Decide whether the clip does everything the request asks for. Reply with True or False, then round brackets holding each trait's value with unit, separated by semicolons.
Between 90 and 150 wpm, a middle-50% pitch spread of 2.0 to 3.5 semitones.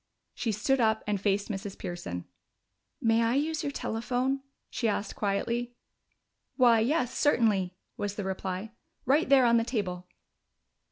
False (145 wpm; 3.9 semitones)